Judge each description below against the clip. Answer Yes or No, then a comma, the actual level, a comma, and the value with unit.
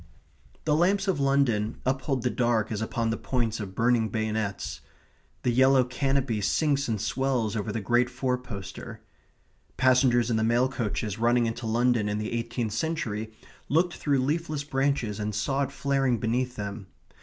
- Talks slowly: No, average, 165 wpm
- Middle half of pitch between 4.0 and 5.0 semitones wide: No, average, 3.5 semitones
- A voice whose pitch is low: Yes, low, 120 Hz